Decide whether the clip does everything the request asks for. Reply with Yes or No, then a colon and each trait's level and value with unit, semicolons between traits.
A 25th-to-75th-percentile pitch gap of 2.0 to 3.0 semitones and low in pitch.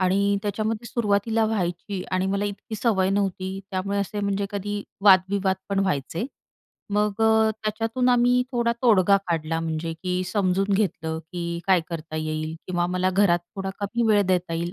No: narrow, 2.5 semitones; high, 195 Hz